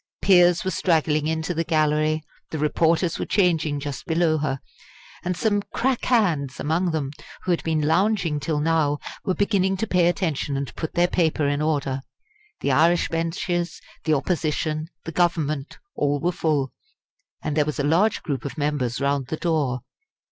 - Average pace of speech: Yes, average, 170 wpm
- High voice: No, medium, 160 Hz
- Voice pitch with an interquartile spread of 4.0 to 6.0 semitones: No, average, 3.0 semitones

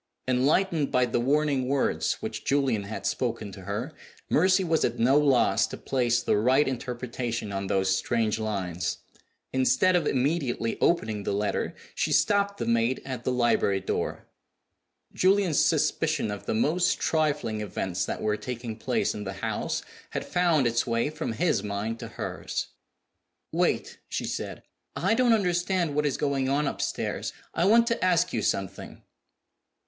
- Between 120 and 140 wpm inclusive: No, average, 160 wpm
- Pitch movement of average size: No, wide, 6.1 semitones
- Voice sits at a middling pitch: No, low, 130 Hz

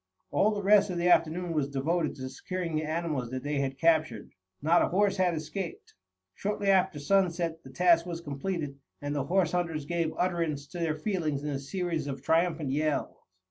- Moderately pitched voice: Yes, medium, 165 Hz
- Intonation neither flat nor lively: Yes, average, 3.6 semitones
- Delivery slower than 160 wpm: No, average, 190 wpm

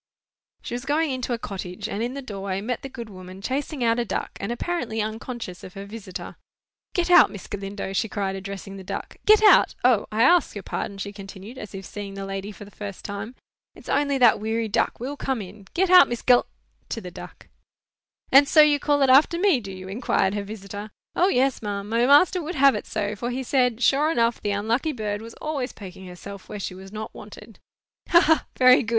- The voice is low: No, high, 225 Hz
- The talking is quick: Yes, fast, 225 wpm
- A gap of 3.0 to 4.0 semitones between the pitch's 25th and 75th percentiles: No, average, 5.2 semitones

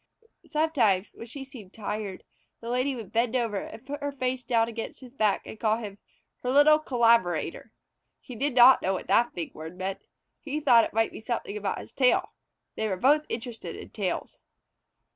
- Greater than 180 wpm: Yes, average, 190 wpm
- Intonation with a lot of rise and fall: No, average, 4.0 semitones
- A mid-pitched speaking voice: No, high, 235 Hz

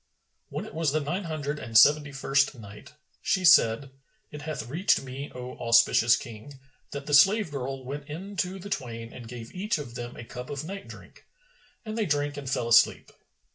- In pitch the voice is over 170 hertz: No, medium, 140 Hz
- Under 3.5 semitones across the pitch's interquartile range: No, average, 4.3 semitones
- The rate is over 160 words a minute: Yes, average, 195 wpm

